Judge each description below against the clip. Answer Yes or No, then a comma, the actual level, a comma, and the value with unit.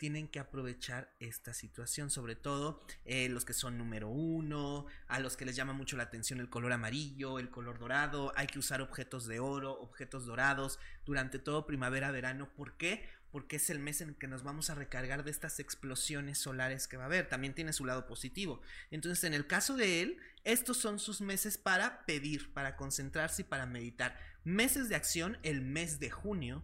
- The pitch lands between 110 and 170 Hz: Yes, medium, 140 Hz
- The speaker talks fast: Yes, fast, 200 wpm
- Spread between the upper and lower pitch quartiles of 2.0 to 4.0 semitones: Yes, average, 3.2 semitones